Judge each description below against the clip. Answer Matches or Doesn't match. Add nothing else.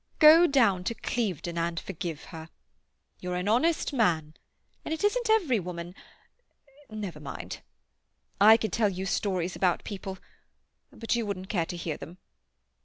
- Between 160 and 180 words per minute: Doesn't match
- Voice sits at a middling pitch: Doesn't match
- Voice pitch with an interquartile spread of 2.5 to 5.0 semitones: Doesn't match